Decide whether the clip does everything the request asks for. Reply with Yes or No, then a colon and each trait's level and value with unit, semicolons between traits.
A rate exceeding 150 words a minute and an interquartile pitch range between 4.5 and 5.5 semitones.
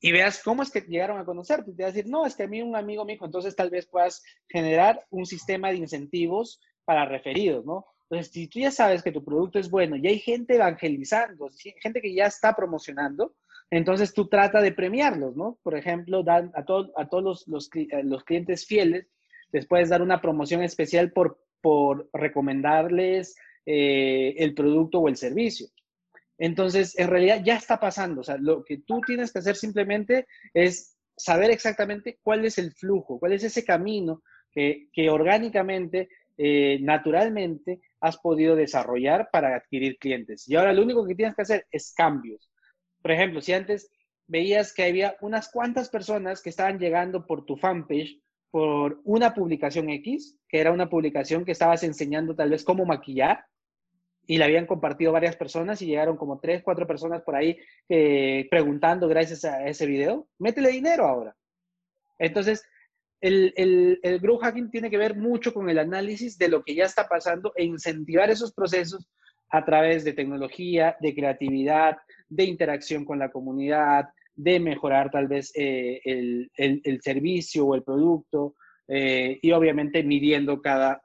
Yes: average, 175 wpm; average, 4.8 semitones